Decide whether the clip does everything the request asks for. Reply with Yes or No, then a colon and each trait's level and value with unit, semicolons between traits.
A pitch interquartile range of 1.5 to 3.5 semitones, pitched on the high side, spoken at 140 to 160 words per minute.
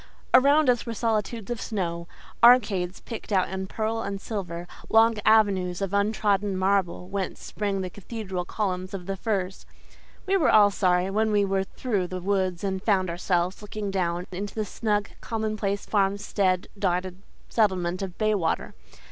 Yes: average, 2.7 semitones; high, 195 Hz; average, 155 wpm